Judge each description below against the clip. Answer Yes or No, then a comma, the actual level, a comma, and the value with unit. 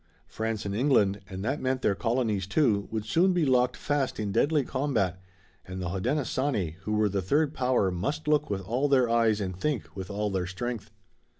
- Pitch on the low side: Yes, low, 110 Hz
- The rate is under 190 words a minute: No, average, 195 wpm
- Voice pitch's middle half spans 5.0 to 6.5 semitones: Yes, average, 5.3 semitones